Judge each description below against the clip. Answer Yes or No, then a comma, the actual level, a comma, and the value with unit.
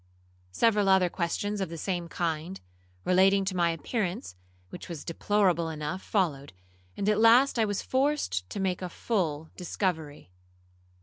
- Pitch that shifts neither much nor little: Yes, average, 3.8 semitones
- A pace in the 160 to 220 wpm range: No, average, 145 wpm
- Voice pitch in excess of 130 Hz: Yes, medium, 185 Hz